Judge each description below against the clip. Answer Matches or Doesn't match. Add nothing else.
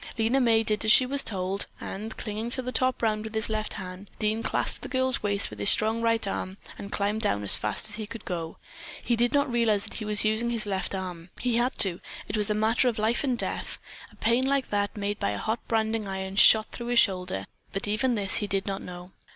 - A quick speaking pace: Matches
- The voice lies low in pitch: Doesn't match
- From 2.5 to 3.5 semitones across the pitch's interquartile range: Matches